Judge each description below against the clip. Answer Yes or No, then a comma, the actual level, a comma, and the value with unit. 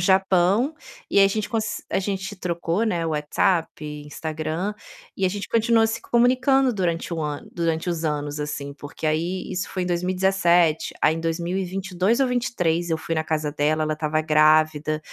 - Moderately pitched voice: Yes, medium, 170 Hz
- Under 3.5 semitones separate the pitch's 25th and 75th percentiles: No, average, 3.8 semitones